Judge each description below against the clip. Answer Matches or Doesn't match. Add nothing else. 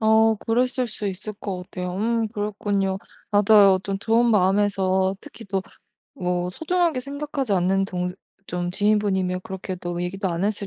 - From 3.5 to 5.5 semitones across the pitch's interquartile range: Doesn't match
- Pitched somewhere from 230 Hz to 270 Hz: Doesn't match